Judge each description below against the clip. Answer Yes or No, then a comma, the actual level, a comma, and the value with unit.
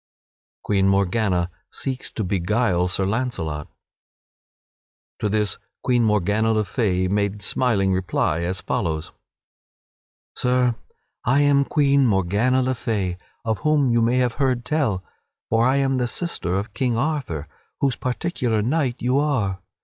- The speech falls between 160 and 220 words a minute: No, average, 140 wpm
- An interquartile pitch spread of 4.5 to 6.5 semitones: Yes, average, 5.0 semitones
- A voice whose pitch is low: Yes, low, 115 Hz